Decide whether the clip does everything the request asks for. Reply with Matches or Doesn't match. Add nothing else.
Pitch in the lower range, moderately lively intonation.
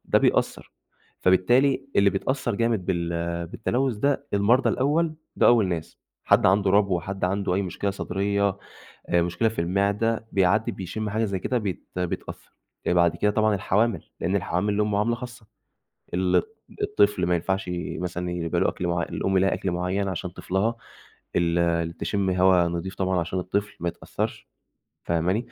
Matches